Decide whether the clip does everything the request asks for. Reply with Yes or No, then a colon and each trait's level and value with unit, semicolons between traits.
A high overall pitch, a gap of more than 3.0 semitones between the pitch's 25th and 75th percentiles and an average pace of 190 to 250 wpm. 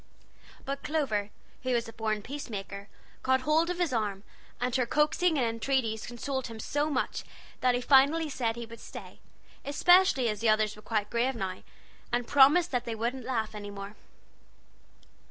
No: high, 245 Hz; average, 4.1 semitones; average, 175 wpm